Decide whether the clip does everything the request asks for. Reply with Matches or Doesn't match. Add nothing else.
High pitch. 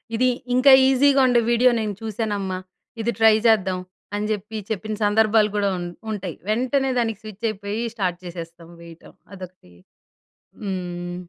Matches